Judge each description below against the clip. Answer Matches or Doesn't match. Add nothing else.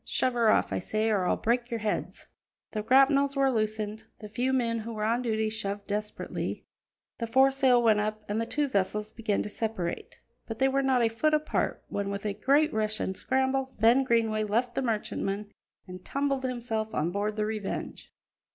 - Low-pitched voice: Doesn't match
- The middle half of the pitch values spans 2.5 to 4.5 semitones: Matches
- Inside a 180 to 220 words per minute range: Matches